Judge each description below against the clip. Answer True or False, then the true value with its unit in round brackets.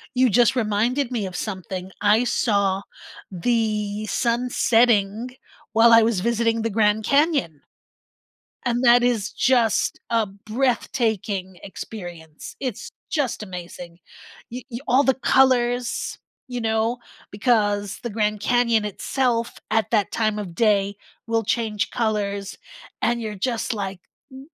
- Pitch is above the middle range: True (220 Hz)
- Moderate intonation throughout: True (3.0 semitones)